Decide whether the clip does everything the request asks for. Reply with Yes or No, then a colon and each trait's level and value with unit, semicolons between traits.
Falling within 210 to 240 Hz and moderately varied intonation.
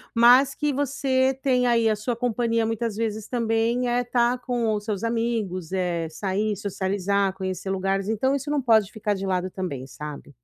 Yes: high, 220 Hz; average, 4.0 semitones